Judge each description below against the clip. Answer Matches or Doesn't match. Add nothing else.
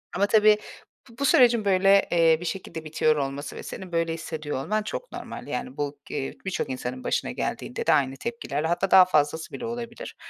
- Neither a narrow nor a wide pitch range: Doesn't match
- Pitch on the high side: Doesn't match